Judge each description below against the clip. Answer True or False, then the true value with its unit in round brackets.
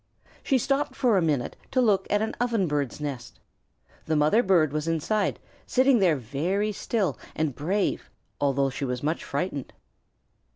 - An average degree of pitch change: False (6.9 semitones)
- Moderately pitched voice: True (165 Hz)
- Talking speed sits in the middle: True (155 wpm)